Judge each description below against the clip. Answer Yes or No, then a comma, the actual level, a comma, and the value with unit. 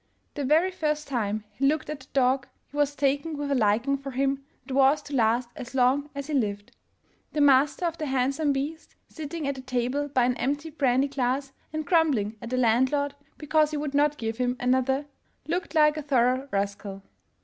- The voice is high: Yes, very high, 275 Hz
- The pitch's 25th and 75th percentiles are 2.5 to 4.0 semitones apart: Yes, average, 2.8 semitones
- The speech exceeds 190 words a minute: Yes, average, 200 wpm